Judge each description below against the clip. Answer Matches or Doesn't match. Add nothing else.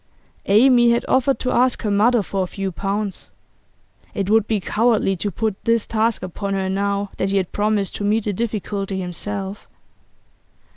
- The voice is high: Matches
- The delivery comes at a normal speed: Matches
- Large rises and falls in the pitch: Doesn't match